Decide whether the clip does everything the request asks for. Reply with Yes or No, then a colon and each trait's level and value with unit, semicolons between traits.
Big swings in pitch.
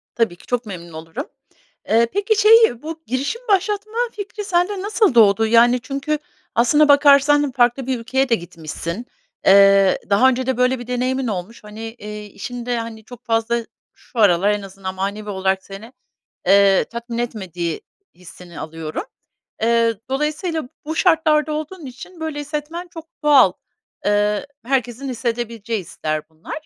Yes: wide, 6.3 semitones